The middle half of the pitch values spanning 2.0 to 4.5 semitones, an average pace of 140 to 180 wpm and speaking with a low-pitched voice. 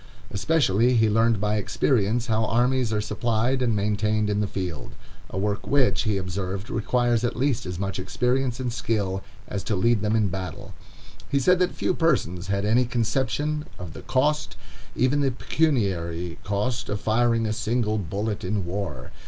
Yes: average, 3.8 semitones; average, 170 wpm; low, 110 Hz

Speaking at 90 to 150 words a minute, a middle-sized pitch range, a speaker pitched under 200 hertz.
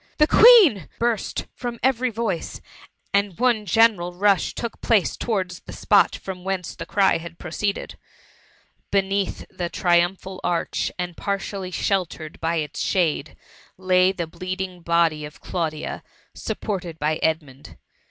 Yes: slow, 135 wpm; average, 3.1 semitones; medium, 185 Hz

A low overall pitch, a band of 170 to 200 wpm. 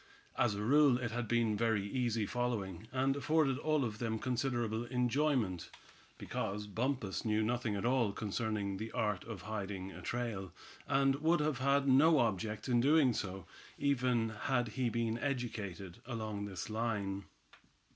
No: low, 115 Hz; average, 155 wpm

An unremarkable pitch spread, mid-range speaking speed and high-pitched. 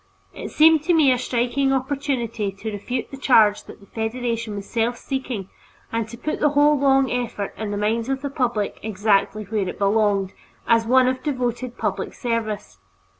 Yes: average, 3.9 semitones; average, 180 wpm; high, 235 Hz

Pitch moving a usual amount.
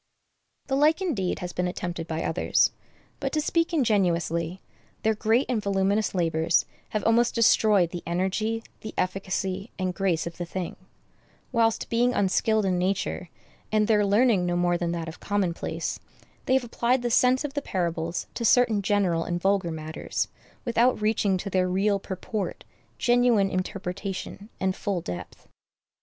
Yes: average, 4.2 semitones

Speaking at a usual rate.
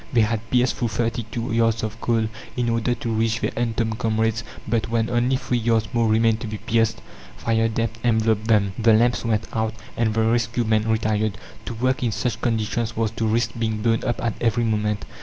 No: fast, 210 wpm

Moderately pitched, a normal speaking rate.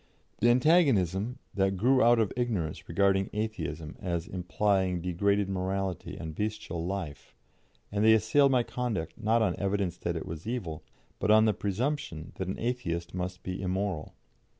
No: low, 100 Hz; average, 155 wpm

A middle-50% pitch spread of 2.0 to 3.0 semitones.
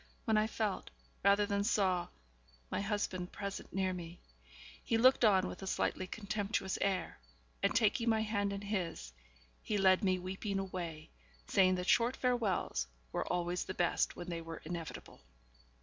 Yes: average, 2.7 semitones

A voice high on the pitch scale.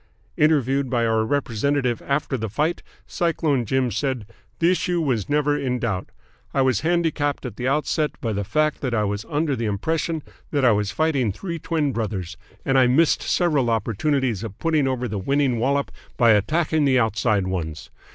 No: low, 130 Hz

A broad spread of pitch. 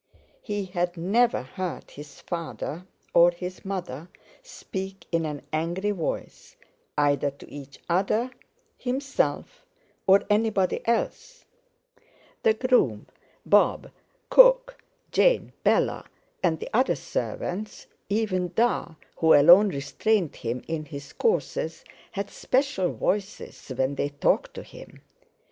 Yes: wide, 5.9 semitones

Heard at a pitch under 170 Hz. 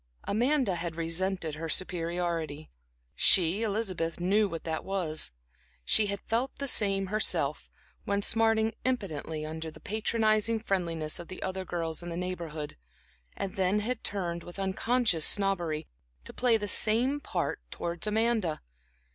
No: high, 190 Hz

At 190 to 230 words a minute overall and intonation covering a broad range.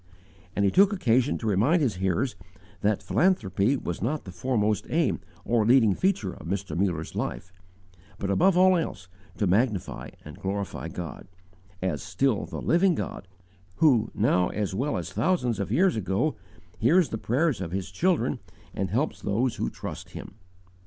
No: average, 165 wpm; wide, 7.1 semitones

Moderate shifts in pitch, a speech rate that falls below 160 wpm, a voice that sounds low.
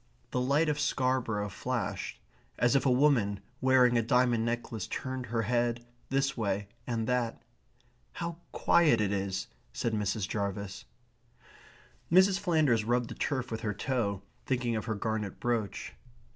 Yes: average, 3.5 semitones; average, 145 wpm; low, 120 Hz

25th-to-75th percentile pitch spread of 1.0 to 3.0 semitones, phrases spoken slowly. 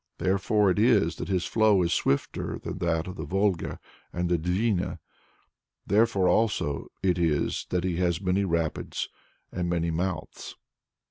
No: average, 2.7 semitones; average, 150 wpm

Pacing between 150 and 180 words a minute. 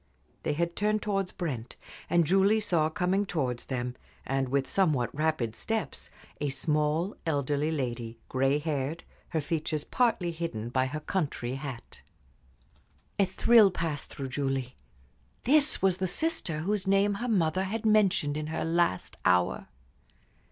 No: average, 140 wpm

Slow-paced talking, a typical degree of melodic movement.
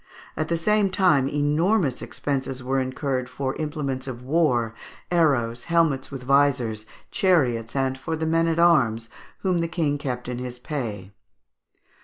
No: average, 150 wpm; average, 4.5 semitones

